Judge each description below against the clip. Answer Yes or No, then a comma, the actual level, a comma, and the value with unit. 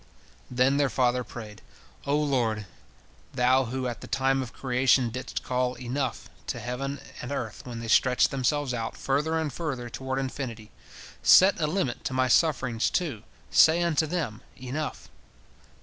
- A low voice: Yes, low, 130 Hz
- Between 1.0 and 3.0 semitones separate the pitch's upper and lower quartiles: Yes, narrow, 2.6 semitones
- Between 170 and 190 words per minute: No, average, 155 wpm